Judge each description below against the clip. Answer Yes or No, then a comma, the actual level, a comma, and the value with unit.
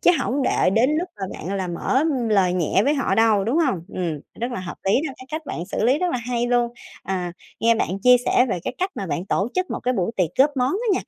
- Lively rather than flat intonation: Yes, wide, 5.9 semitones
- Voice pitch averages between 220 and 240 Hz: Yes, high, 235 Hz